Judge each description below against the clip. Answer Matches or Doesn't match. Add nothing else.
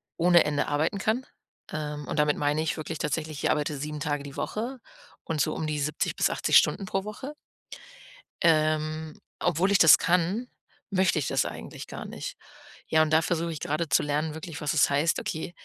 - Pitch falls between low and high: Matches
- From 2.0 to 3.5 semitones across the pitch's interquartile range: Matches